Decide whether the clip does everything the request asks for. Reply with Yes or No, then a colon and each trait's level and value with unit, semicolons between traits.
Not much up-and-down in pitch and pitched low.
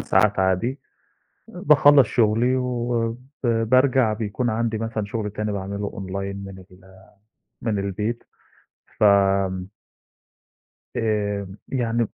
No: average, 3.2 semitones; low, 105 Hz